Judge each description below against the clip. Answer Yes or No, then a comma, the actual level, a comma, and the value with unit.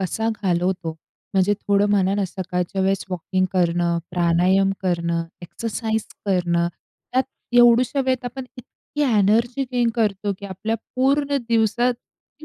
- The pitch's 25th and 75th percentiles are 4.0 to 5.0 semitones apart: Yes, average, 4.7 semitones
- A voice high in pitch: Yes, high, 200 Hz